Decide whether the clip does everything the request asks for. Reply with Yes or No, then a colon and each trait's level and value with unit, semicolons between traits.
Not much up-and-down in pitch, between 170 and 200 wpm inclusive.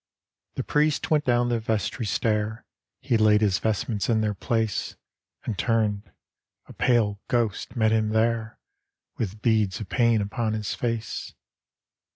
No: narrow, 1.8 semitones; average, 150 wpm